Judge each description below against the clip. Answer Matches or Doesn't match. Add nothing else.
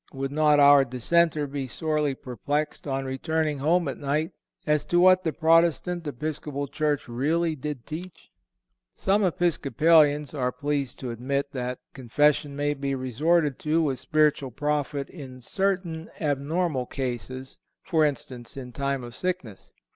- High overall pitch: Doesn't match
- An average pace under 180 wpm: Matches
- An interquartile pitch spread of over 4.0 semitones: Doesn't match